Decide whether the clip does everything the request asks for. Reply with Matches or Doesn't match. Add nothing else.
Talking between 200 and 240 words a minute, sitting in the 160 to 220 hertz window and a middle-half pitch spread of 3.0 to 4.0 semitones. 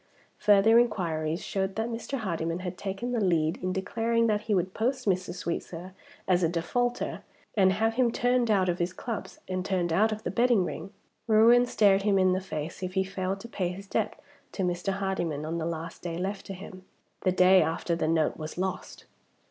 Matches